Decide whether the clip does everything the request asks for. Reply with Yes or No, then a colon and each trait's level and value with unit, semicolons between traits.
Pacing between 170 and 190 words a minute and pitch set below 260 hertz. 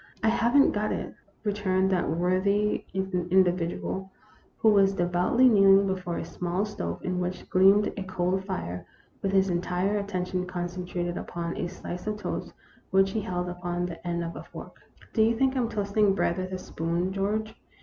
Yes: average, 180 wpm; medium, 185 Hz